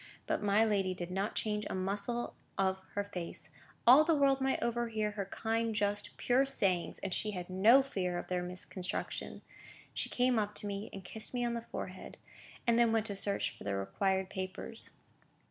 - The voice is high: Yes, high, 205 Hz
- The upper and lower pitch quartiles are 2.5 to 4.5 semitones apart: Yes, average, 3.6 semitones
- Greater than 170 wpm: Yes, average, 190 wpm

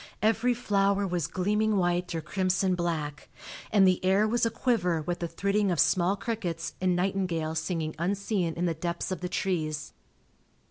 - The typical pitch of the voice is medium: Yes, medium, 180 Hz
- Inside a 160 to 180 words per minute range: Yes, average, 165 wpm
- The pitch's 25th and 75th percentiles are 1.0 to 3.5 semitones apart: Yes, average, 3.0 semitones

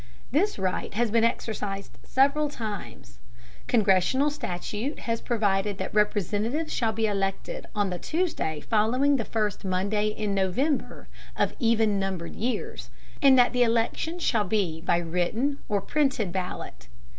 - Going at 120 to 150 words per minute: Yes, average, 140 wpm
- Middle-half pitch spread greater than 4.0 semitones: Yes, average, 4.6 semitones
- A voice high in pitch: Yes, high, 215 Hz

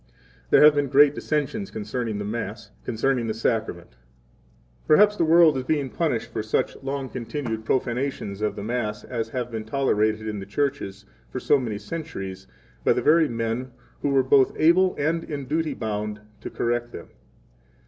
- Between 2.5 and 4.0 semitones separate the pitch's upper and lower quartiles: No, average, 5.0 semitones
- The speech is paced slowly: No, average, 180 wpm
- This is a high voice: No, low, 125 Hz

